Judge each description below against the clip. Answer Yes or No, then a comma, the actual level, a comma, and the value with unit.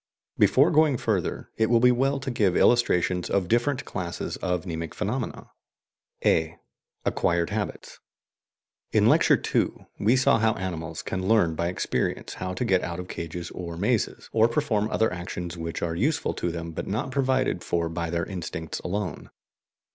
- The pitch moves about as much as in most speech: No, wide, 5.7 semitones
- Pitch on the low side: Yes, very low, 95 Hz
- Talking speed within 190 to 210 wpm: No, average, 165 wpm